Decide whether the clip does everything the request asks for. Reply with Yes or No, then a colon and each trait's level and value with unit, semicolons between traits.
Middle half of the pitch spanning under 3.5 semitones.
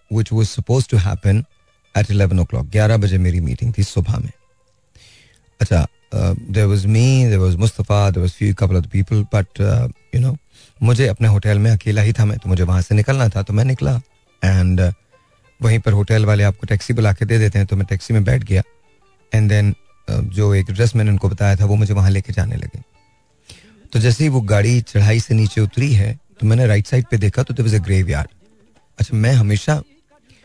Yes: average, 2.7 semitones